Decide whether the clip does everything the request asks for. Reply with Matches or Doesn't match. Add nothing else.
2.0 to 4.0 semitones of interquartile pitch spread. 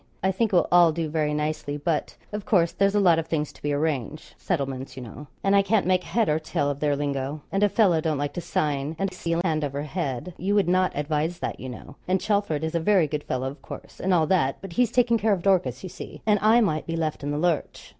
Doesn't match